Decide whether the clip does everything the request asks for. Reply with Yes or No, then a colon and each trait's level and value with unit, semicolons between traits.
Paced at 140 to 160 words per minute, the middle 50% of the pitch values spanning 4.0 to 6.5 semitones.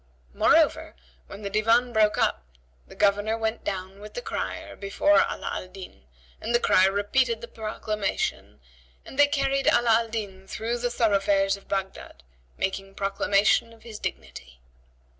No: average, 155 wpm; average, 2.9 semitones